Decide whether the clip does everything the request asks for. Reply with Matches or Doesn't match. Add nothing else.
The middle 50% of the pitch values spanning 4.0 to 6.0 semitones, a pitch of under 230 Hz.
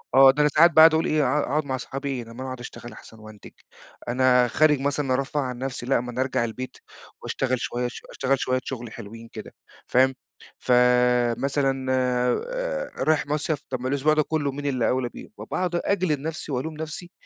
Doesn't match